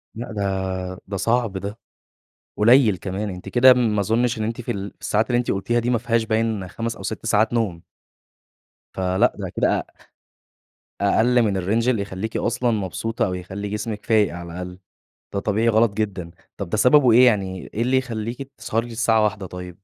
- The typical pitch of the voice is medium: No, low, 110 Hz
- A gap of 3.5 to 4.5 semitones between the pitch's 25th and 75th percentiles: No, average, 3.1 semitones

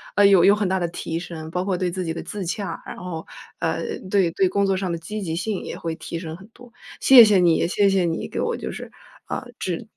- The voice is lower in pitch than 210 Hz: Yes, medium, 185 Hz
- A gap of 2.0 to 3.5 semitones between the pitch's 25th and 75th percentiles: Yes, average, 2.9 semitones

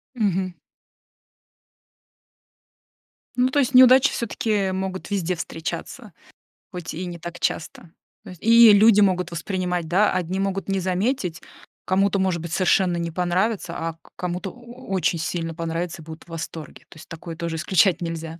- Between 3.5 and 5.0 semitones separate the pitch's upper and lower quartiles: No, average, 2.9 semitones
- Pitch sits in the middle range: Yes, medium, 180 Hz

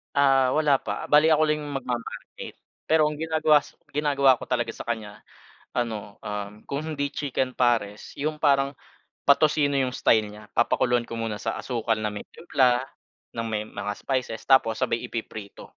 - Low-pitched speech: Yes, low, 125 Hz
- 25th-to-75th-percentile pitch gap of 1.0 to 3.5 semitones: No, average, 4.3 semitones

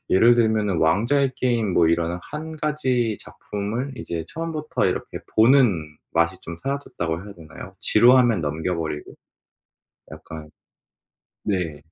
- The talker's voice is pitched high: No, low, 105 Hz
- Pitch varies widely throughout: Yes, wide, 7.4 semitones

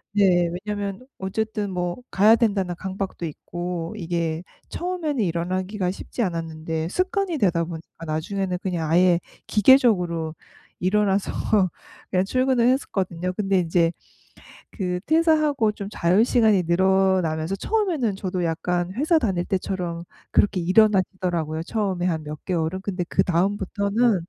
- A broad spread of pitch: No, average, 3.5 semitones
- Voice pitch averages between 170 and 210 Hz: Yes, high, 190 Hz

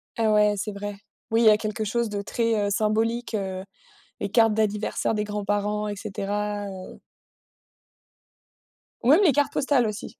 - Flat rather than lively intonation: Yes, narrow, 1.7 semitones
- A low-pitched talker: No, high, 210 Hz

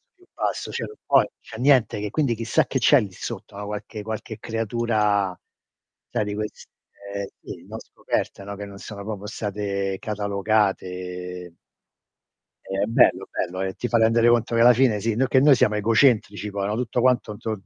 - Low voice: Yes, low, 105 Hz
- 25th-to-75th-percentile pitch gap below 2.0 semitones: No, narrow, 2.6 semitones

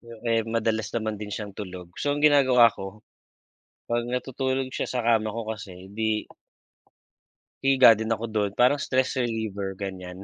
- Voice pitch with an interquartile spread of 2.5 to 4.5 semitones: Yes, average, 3.2 semitones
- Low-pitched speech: Yes, low, 110 Hz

